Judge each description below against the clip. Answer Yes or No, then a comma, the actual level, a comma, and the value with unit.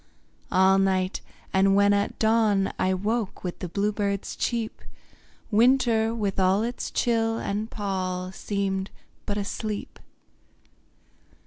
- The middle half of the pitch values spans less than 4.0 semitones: Yes, narrow, 2.4 semitones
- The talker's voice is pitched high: Yes, high, 200 Hz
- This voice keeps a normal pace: No, slow, 125 wpm